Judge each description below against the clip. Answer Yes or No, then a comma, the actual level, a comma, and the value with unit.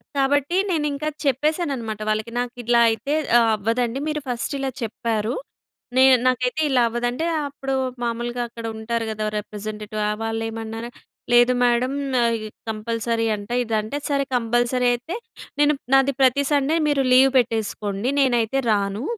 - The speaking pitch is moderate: No, high, 240 Hz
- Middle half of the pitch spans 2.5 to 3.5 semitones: Yes, average, 3.2 semitones